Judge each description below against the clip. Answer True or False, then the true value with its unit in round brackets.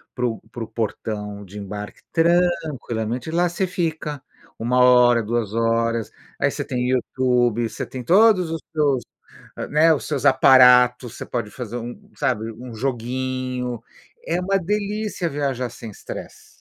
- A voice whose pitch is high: False (125 Hz)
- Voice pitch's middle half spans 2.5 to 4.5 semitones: False (5.0 semitones)